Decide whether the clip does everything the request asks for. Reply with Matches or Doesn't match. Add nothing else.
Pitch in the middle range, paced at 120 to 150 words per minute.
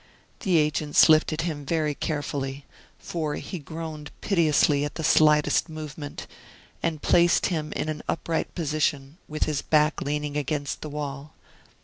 Matches